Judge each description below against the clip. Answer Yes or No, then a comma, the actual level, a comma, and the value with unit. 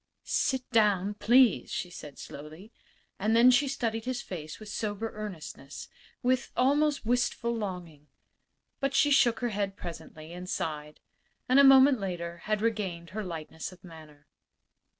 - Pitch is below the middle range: No, high, 210 Hz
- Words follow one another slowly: No, average, 150 wpm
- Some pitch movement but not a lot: No, wide, 6.3 semitones